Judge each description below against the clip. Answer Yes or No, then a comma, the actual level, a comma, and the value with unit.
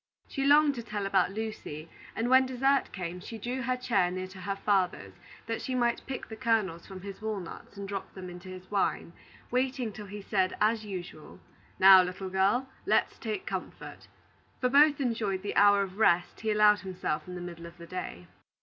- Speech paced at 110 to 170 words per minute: No, average, 195 wpm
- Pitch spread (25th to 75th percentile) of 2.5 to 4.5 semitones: Yes, average, 4.2 semitones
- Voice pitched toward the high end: Yes, high, 200 Hz